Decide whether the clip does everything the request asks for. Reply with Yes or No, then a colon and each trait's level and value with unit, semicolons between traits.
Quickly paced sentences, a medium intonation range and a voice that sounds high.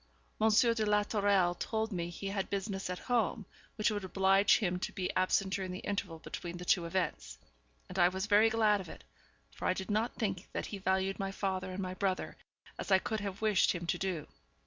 No: fast, 215 wpm; narrow, 2.1 semitones; high, 195 Hz